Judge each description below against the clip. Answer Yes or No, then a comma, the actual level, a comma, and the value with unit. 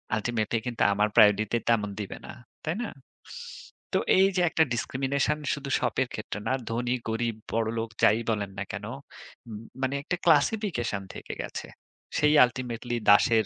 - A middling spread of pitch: Yes, average, 4.2 semitones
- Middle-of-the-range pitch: No, low, 120 Hz